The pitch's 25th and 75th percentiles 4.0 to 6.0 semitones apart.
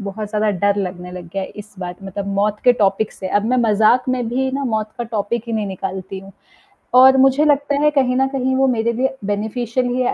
Yes: average, 4.3 semitones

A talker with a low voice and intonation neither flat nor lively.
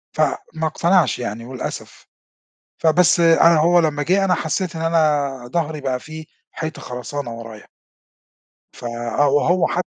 No: medium, 155 Hz; average, 3.5 semitones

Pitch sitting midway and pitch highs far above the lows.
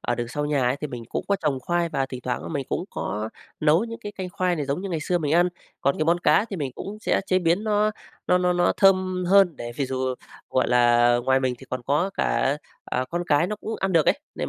Yes: medium, 160 Hz; wide, 5.9 semitones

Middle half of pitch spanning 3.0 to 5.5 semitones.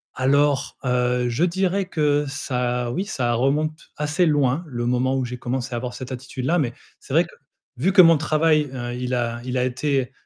Yes: average, 3.5 semitones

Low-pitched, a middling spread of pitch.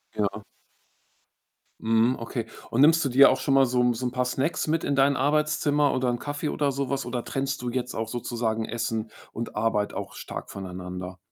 Yes: low, 125 Hz; average, 3.5 semitones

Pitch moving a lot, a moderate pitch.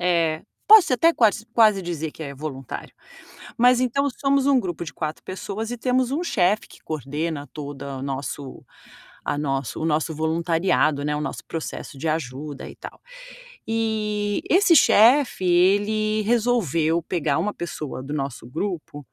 Yes: wide, 6.7 semitones; medium, 170 Hz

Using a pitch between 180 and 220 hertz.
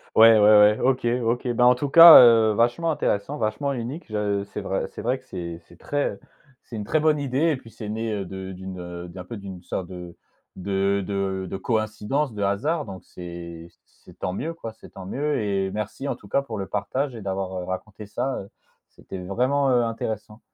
No: low, 105 Hz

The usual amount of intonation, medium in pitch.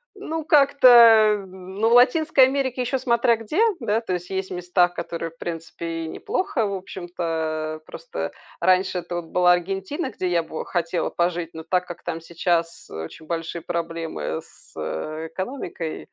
No: wide, 5.7 semitones; medium, 180 Hz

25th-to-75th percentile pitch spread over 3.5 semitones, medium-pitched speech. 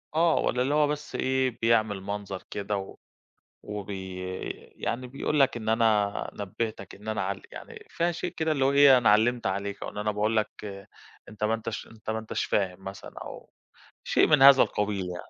No: average, 4.4 semitones; low, 110 Hz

